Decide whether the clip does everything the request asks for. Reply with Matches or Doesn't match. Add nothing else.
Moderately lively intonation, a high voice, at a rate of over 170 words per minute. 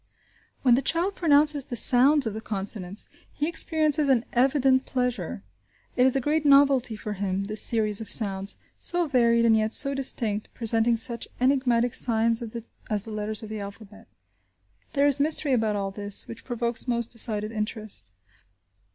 Doesn't match